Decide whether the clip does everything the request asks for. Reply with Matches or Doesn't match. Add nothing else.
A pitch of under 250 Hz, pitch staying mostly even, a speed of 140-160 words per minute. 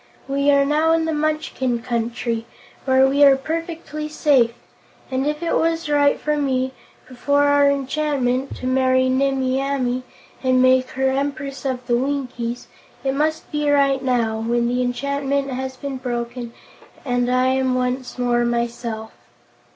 Doesn't match